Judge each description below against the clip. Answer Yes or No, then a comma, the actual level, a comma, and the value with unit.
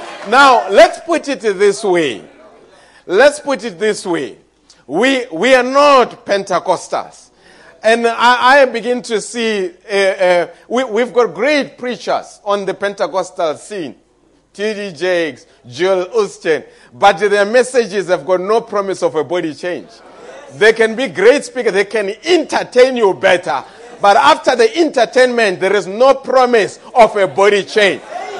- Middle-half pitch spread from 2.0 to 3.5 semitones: No, average, 5.3 semitones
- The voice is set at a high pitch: Yes, high, 220 Hz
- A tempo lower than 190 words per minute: Yes, average, 150 wpm